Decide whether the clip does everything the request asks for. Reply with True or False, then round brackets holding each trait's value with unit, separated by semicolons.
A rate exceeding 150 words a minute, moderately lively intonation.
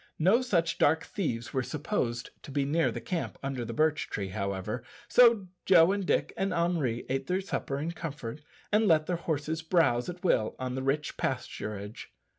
False (185 wpm; 6.0 semitones)